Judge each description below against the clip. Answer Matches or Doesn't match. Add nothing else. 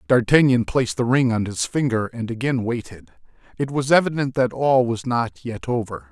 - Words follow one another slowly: Doesn't match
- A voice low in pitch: Matches